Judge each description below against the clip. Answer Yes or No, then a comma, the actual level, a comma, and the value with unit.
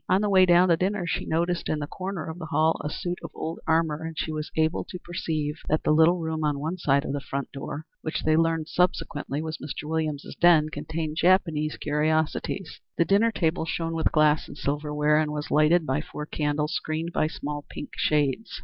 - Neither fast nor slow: No, fast, 215 wpm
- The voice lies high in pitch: No, medium, 160 Hz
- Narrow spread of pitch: Yes, narrow, 2.0 semitones